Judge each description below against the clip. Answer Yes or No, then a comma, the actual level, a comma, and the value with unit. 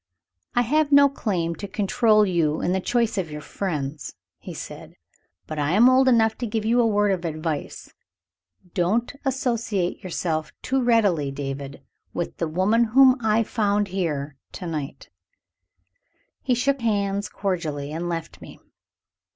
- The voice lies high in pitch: Yes, high, 195 Hz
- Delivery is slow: No, average, 150 wpm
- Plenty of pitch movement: Yes, wide, 6.1 semitones